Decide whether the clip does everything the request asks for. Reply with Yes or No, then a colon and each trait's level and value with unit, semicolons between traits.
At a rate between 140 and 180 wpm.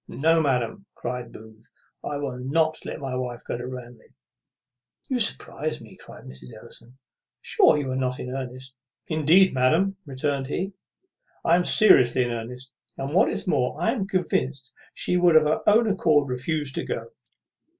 Yes: average, 170 wpm